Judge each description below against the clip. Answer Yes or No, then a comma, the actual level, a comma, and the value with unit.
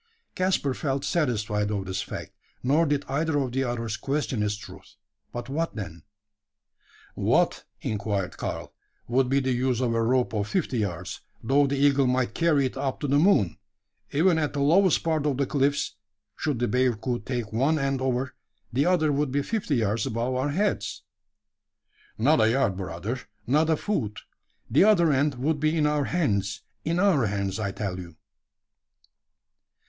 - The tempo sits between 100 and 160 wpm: No, average, 175 wpm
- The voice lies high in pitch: No, low, 130 Hz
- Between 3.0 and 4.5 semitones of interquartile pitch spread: No, average, 5.2 semitones